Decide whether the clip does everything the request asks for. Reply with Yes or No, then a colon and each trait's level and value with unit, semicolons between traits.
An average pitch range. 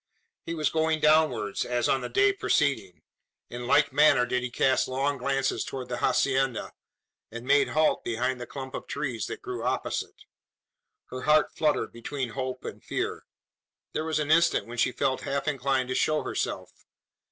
Yes: average, 3.4 semitones